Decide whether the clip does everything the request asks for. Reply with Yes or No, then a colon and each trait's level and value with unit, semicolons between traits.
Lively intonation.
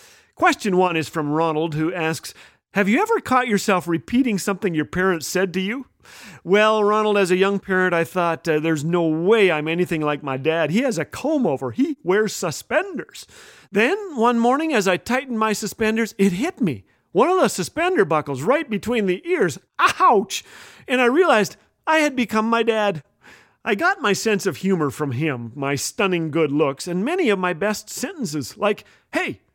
Yes: wide, 6.2 semitones